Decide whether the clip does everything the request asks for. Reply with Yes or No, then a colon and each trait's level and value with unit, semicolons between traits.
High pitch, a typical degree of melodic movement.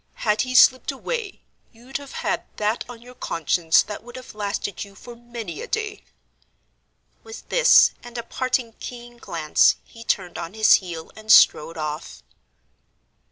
Yes: high, 230 Hz; average, 5.0 semitones